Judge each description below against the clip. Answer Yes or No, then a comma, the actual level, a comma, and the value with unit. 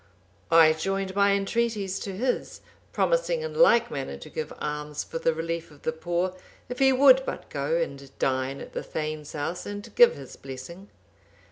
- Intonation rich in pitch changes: Yes, wide, 6.2 semitones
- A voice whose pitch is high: No, medium, 175 Hz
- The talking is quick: No, average, 175 wpm